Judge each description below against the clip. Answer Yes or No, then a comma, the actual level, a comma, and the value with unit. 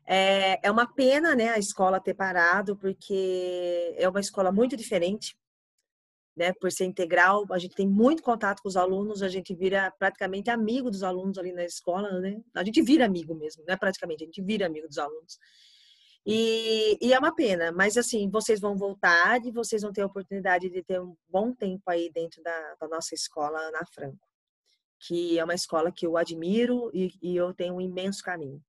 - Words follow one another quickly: Yes, fast, 195 wpm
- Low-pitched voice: No, high, 190 Hz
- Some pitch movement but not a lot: Yes, average, 3.3 semitones